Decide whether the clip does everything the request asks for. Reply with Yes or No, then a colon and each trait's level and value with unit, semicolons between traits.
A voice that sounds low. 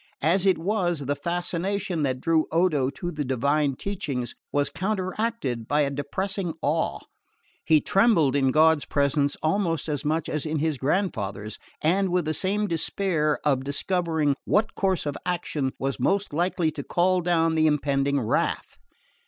No: medium, 160 Hz